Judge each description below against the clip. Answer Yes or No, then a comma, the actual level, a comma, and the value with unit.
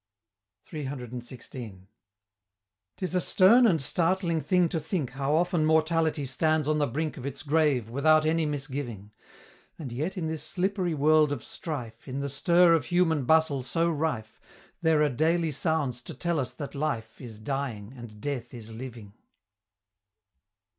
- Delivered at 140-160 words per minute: Yes, average, 155 wpm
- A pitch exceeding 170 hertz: No, medium, 150 Hz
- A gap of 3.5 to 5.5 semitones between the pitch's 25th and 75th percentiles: Yes, average, 4.2 semitones